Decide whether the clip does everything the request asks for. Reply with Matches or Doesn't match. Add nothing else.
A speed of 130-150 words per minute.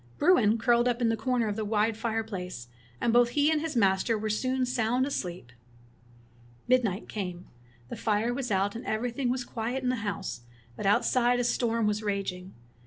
Doesn't match